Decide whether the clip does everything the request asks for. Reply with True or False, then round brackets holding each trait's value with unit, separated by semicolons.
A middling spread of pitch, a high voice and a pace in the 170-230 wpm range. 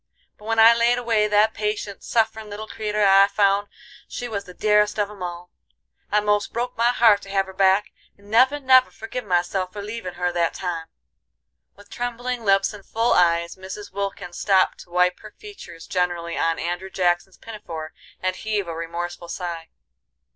True (3.4 semitones; 200 Hz; 180 wpm)